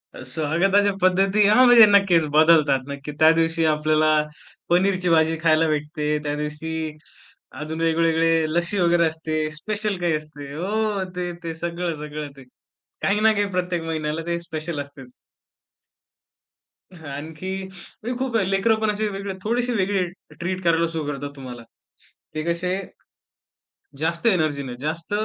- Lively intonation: No, average, 3.6 semitones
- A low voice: No, medium, 165 Hz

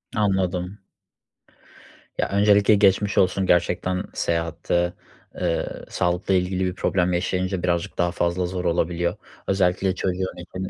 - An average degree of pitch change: No, narrow, 1.5 semitones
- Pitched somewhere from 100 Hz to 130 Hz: No, very low, 90 Hz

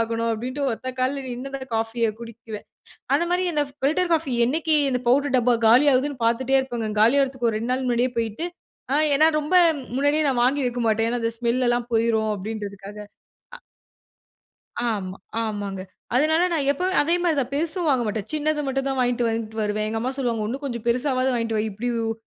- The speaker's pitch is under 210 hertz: No, high, 245 Hz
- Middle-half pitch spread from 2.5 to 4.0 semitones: Yes, average, 3.7 semitones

